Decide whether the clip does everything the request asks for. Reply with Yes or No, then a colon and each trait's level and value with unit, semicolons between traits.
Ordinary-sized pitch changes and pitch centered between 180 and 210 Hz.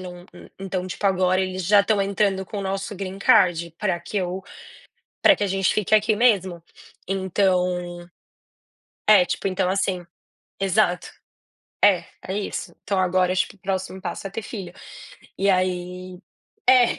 No: narrow, 1.6 semitones; high, 190 Hz